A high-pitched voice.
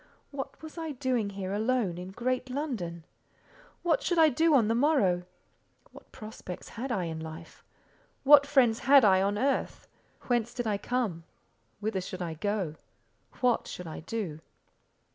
Yes: high, 225 Hz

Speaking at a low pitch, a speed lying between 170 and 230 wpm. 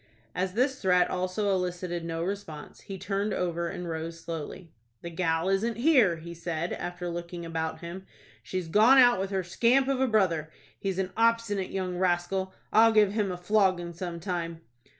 No: medium, 185 Hz; average, 175 wpm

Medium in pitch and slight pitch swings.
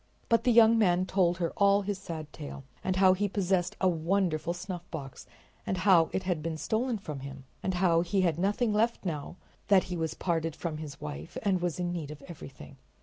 No: medium, 180 Hz; average, 3.4 semitones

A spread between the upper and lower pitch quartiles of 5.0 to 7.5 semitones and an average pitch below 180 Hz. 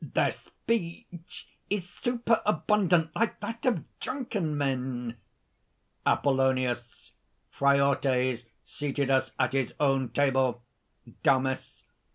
Yes: average, 5.3 semitones; medium, 140 Hz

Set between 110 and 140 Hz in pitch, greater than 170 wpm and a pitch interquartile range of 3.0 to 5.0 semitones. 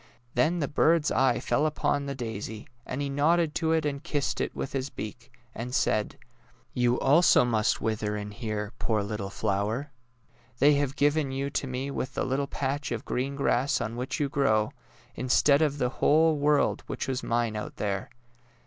Yes: low, 135 Hz; average, 185 wpm; average, 4.2 semitones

